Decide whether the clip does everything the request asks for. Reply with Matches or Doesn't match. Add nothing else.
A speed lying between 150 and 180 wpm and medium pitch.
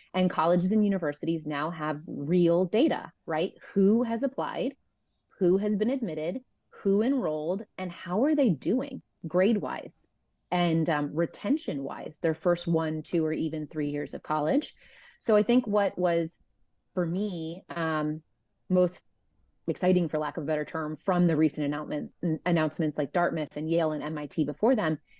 Matches